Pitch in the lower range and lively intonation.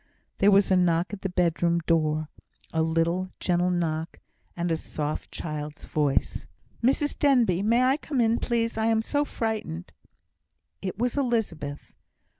No: medium, 180 Hz; wide, 5.9 semitones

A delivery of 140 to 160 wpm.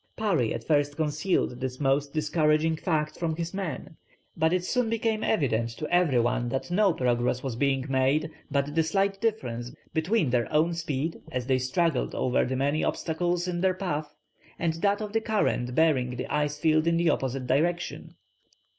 No: average, 180 wpm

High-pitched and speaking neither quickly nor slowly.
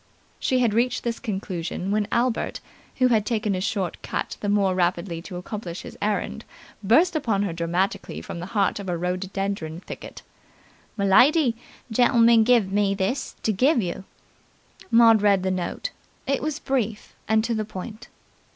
Yes: high, 205 Hz; average, 160 wpm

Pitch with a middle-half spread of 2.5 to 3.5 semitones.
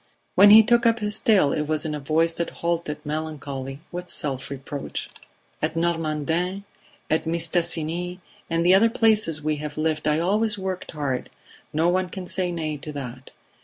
Yes: average, 3.2 semitones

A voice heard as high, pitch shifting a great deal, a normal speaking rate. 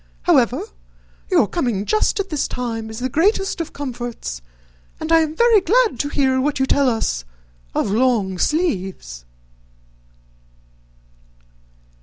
No: very high, 260 Hz; wide, 6.8 semitones; slow, 130 wpm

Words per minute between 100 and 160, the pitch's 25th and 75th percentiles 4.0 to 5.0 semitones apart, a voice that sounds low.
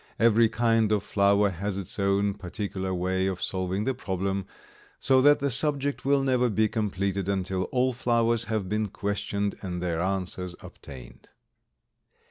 No: average, 150 wpm; average, 3.5 semitones; low, 100 Hz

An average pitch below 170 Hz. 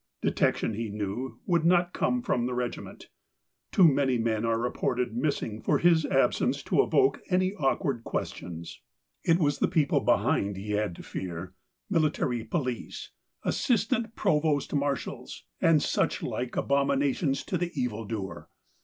Yes: low, 135 Hz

